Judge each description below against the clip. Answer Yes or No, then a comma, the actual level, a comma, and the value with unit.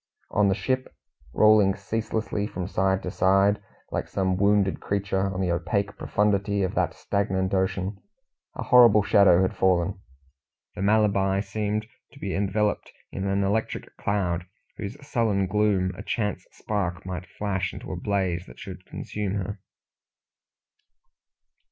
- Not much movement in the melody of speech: Yes, narrow, 1.6 semitones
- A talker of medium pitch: No, low, 100 Hz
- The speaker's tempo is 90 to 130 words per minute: No, average, 140 wpm